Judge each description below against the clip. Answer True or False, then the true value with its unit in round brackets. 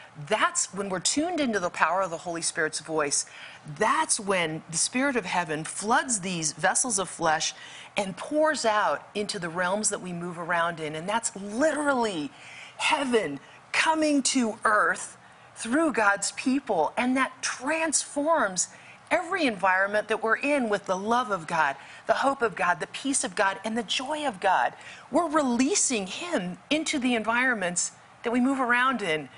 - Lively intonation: True (7.4 semitones)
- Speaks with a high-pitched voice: True (220 Hz)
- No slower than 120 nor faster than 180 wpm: True (165 wpm)